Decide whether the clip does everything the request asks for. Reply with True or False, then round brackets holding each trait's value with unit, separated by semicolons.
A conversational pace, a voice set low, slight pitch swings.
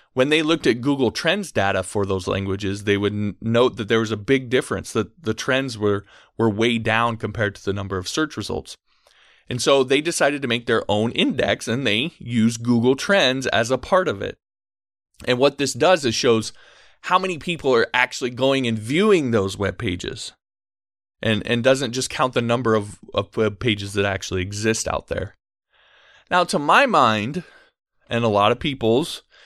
False (190 wpm; 115 Hz; 4.2 semitones)